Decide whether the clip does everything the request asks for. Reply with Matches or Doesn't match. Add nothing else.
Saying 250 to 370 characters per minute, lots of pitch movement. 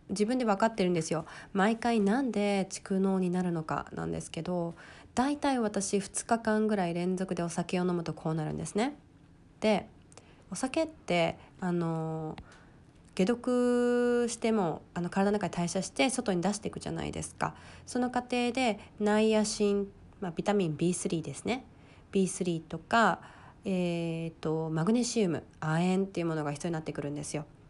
Doesn't match